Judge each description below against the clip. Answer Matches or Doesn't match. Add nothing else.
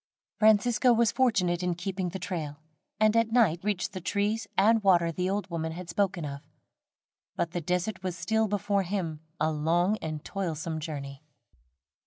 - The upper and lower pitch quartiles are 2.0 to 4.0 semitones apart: Matches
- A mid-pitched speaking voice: Matches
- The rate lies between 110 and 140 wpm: Doesn't match